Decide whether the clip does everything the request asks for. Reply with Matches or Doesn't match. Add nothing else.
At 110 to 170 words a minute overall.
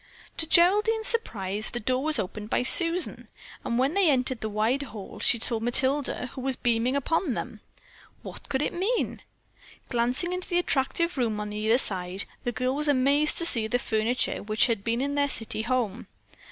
Doesn't match